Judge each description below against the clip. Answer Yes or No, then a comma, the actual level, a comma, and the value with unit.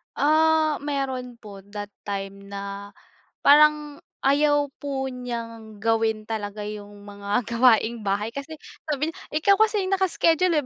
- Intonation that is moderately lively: No, wide, 6.4 semitones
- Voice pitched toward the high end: Yes, high, 245 Hz